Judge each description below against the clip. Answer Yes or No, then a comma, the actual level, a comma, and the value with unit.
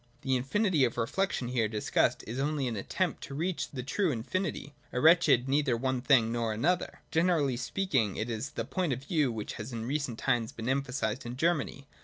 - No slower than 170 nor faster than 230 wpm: Yes, average, 195 wpm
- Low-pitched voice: Yes, low, 130 Hz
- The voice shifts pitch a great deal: No, average, 4.5 semitones